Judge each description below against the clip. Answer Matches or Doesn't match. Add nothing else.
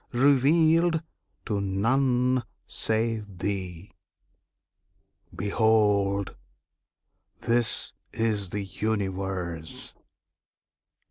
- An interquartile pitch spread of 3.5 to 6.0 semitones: Matches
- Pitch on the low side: Matches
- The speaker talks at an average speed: Doesn't match